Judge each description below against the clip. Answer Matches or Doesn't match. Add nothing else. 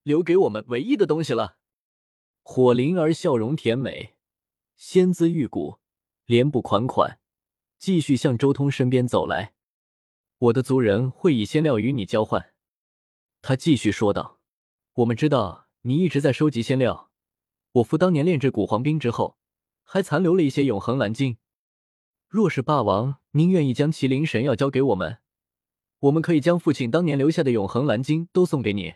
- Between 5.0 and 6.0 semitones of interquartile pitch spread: Matches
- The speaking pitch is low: Matches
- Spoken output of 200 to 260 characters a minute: Matches